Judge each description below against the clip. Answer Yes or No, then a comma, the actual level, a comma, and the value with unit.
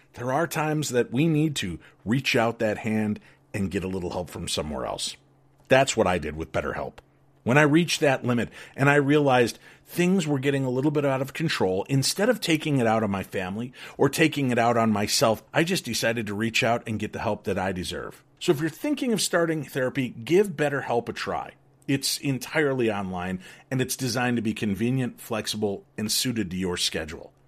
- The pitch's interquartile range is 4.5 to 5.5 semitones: Yes, average, 5.1 semitones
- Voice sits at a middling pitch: No, low, 125 Hz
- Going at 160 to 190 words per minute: No, fast, 205 wpm